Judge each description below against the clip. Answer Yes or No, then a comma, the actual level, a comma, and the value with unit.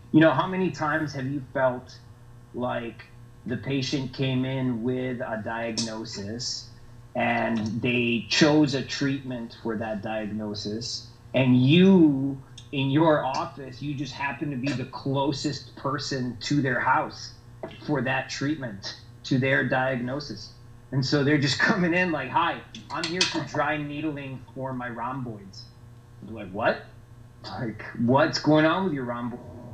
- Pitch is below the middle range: Yes, low, 125 Hz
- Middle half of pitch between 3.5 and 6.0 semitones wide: No, average, 2.9 semitones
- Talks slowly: No, average, 145 wpm